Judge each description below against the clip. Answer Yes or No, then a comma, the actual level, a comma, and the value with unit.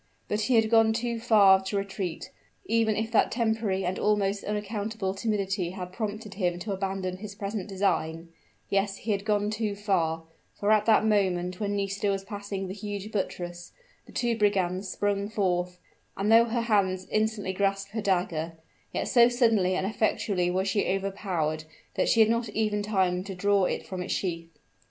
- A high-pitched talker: Yes, high, 200 Hz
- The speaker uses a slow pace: No, average, 180 wpm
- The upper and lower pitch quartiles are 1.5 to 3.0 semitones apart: Yes, narrow, 2.4 semitones